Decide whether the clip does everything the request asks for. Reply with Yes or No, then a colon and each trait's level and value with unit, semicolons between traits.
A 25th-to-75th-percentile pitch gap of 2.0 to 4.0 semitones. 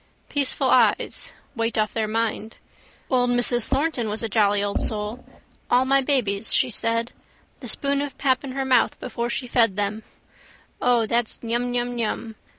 Yes: narrow, 2.6 semitones